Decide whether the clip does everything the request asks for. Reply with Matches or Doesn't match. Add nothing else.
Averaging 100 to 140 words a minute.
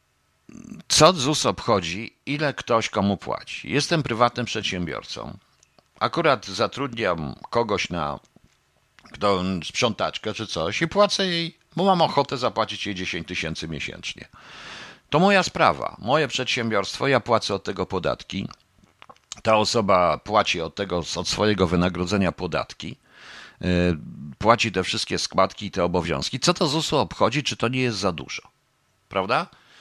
Matches